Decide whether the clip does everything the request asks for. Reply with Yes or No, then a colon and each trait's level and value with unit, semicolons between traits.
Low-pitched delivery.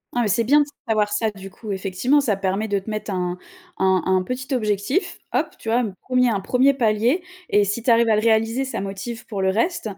No: high, 220 Hz